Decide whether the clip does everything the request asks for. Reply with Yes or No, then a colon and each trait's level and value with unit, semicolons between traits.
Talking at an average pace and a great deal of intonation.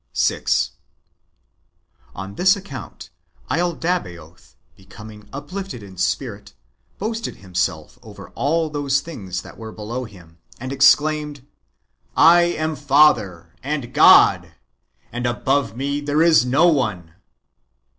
No: slow, 115 wpm; wide, 7.0 semitones